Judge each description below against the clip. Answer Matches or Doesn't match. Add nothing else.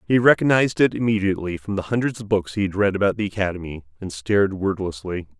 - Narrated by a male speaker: Matches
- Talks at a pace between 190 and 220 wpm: Matches